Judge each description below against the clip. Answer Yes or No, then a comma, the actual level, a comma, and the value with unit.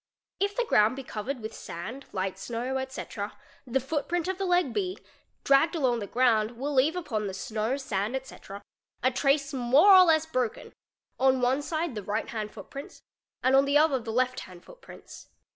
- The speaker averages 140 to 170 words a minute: No, average, 185 wpm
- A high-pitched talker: Yes, very high, 260 Hz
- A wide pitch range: No, average, 4.8 semitones